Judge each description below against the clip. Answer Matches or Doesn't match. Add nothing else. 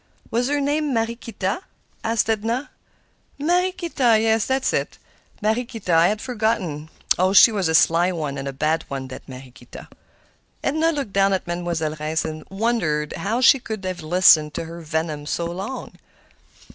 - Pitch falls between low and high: Doesn't match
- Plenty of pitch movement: Matches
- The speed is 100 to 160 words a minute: Matches